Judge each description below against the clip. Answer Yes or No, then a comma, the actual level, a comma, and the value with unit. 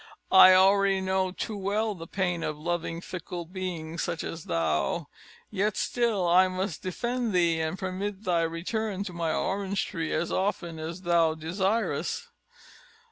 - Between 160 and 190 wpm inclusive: No, average, 150 wpm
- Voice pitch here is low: No, medium, 185 Hz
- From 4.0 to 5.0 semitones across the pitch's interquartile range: No, average, 2.9 semitones